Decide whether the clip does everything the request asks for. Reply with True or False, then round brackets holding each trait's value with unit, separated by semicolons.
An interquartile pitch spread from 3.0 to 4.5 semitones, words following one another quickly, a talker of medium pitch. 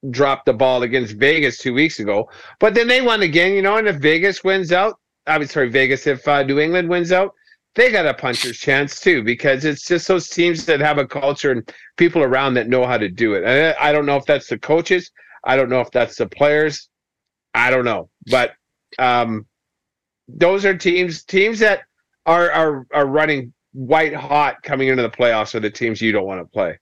False (5.3 semitones; 215 wpm; 150 Hz)